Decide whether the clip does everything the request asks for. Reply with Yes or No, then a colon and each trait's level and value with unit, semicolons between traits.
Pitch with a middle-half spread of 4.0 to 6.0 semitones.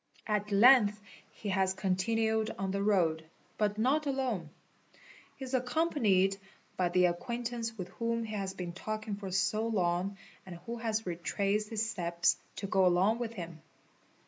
No: average, 3.5 semitones